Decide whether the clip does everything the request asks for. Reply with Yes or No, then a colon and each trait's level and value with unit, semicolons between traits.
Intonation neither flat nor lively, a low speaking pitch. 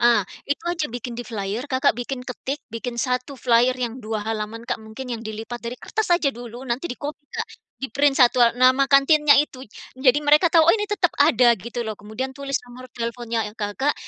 No: average, 3.2 semitones; very high, 250 Hz